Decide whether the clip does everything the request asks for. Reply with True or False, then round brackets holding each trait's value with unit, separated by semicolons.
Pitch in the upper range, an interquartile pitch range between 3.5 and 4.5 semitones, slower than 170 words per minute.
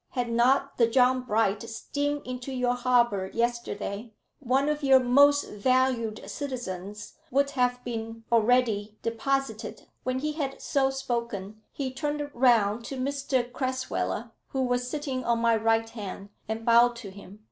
False (245 Hz; 2.9 semitones; 145 wpm)